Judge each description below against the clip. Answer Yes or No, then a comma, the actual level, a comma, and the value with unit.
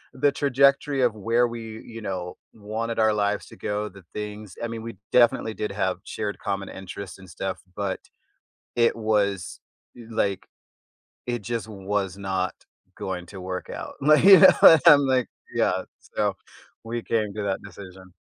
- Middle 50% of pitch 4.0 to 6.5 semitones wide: No, average, 3.2 semitones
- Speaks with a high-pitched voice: No, low, 105 Hz